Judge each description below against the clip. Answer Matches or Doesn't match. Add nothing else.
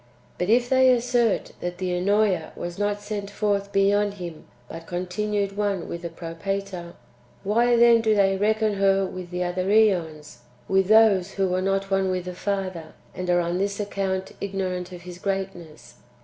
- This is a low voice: Doesn't match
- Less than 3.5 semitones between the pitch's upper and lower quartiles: Matches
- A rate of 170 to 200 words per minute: Matches